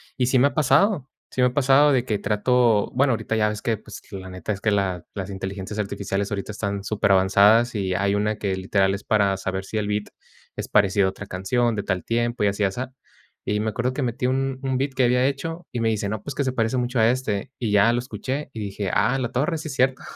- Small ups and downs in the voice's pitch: No, average, 4.3 semitones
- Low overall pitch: Yes, low, 110 Hz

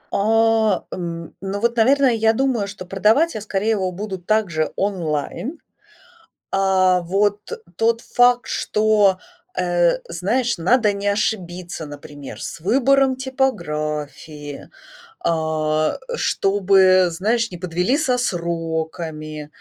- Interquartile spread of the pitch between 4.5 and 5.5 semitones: Yes, average, 4.9 semitones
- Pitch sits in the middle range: No, high, 195 Hz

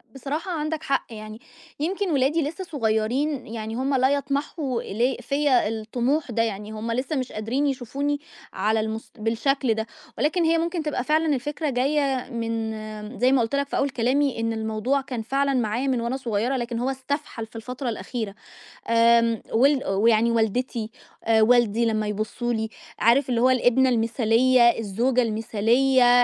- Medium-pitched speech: No, high, 245 Hz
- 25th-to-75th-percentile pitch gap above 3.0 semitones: Yes, average, 3.6 semitones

